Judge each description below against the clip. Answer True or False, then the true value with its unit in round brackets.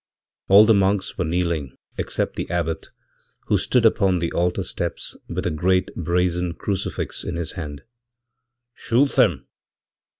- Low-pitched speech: True (90 Hz)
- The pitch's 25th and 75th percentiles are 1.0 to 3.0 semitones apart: True (2.5 semitones)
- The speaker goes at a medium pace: False (130 wpm)